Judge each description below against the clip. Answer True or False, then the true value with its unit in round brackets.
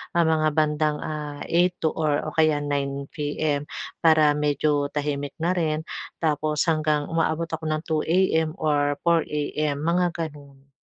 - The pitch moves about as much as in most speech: False (1.6 semitones)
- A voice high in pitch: False (155 Hz)